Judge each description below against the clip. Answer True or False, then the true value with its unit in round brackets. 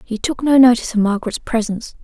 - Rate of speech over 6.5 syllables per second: True (6.9 syllables/s)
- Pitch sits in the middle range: False (230 Hz)